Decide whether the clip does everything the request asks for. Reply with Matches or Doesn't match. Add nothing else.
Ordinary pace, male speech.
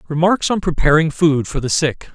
Matches